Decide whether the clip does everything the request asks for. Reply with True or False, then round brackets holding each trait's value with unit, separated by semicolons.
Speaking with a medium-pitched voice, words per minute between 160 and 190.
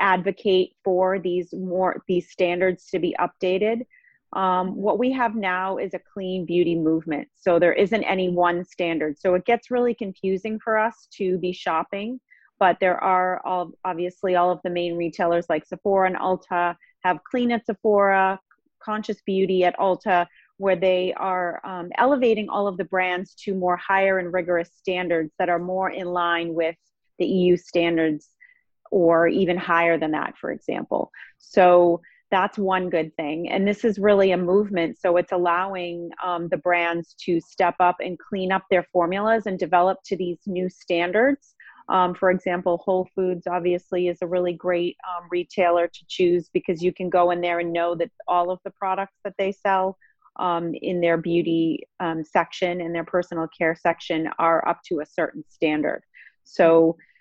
True (180 Hz; 175 wpm)